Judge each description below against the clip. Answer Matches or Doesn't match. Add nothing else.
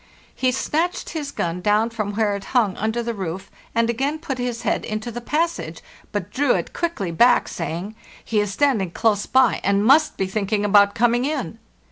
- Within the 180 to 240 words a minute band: Matches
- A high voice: Matches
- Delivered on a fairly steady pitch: Doesn't match